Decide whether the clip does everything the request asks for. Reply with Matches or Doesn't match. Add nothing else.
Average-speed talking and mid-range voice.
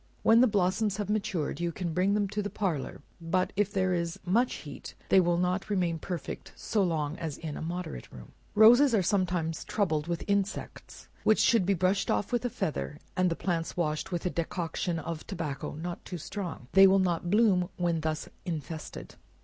Matches